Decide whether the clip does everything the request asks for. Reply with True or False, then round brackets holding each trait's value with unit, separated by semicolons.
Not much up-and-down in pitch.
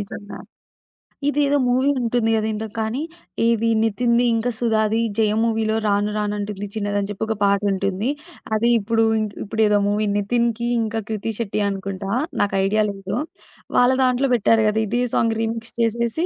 True (2.1 semitones)